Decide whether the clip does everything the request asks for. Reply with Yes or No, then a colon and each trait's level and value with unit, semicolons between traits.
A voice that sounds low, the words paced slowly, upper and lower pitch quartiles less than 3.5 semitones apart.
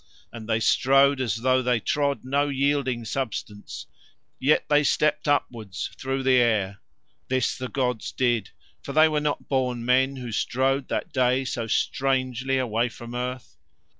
No: low, 130 Hz; average, 155 wpm; narrow, 2.4 semitones